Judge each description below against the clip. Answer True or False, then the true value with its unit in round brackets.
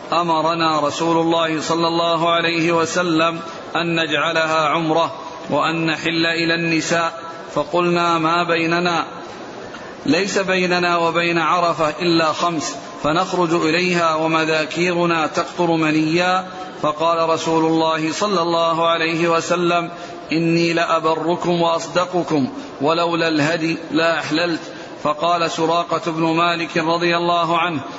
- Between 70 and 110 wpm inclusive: True (105 wpm)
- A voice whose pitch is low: False (165 Hz)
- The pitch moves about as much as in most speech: False (1.0 semitones)